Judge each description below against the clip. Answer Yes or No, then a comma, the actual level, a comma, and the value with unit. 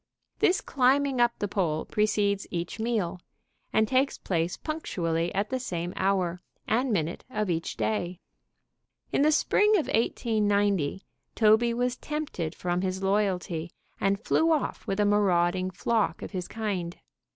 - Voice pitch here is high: Yes, high, 205 Hz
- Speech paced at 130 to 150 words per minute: Yes, average, 145 wpm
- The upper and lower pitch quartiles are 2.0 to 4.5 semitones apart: No, average, 5.0 semitones